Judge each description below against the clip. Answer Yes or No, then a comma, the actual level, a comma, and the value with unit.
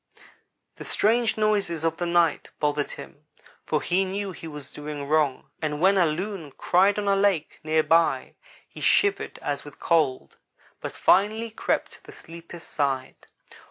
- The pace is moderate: Yes, average, 160 wpm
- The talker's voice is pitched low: No, medium, 170 Hz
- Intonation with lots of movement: No, average, 4.7 semitones